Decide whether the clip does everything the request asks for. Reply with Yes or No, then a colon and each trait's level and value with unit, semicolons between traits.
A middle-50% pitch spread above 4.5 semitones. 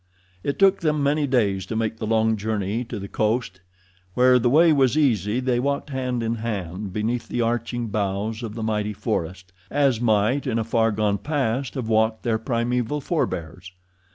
No: average, 3.2 semitones